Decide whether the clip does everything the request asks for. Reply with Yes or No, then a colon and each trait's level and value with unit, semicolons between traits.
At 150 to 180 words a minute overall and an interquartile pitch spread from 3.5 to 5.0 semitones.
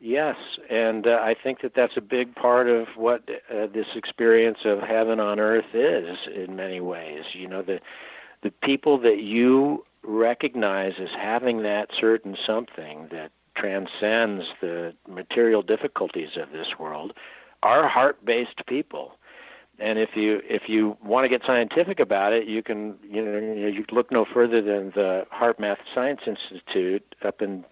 No: average, 160 wpm; narrow, 2.6 semitones